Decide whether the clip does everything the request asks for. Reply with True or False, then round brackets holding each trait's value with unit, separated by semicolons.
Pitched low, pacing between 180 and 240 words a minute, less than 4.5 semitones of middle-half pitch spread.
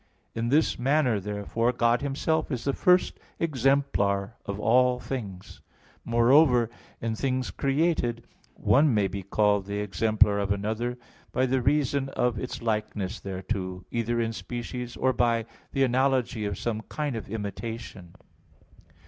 False (120 Hz; 140 wpm; 4.0 semitones)